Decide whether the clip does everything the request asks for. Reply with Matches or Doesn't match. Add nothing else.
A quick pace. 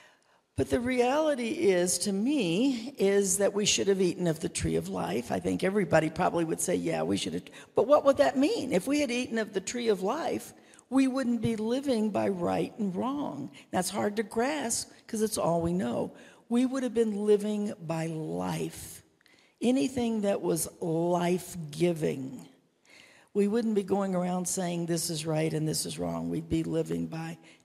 Doesn't match